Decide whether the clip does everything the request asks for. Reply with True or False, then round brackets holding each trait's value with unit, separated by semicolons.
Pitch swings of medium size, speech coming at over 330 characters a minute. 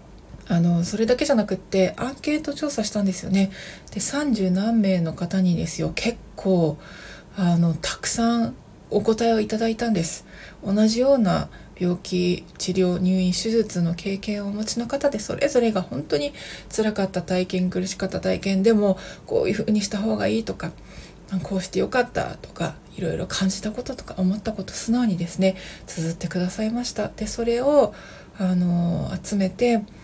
True (3.7 semitones; 340 characters per minute)